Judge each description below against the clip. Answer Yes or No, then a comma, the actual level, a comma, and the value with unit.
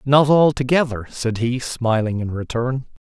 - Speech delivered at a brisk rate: No, slow, 135 wpm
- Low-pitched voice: Yes, low, 125 Hz